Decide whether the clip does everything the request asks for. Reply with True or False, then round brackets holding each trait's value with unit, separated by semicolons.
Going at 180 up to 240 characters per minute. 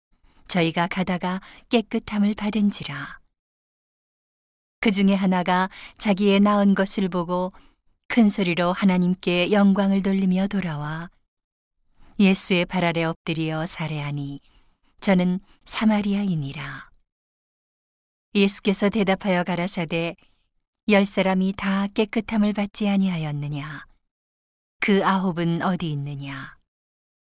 True (235 characters per minute)